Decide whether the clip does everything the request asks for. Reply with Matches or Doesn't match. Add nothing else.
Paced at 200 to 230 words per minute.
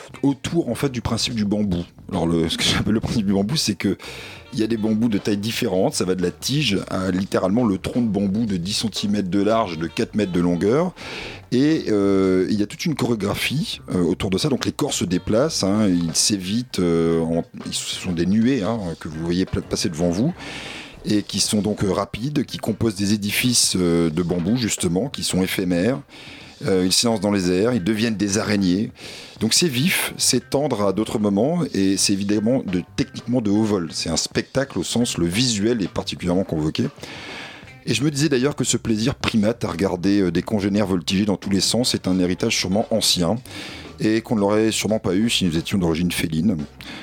Matches